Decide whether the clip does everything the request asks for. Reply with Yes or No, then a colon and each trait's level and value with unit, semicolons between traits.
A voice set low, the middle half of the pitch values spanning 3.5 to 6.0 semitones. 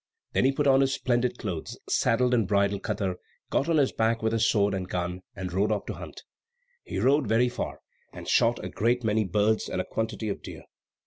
Yes: low, 110 Hz; average, 3.8 semitones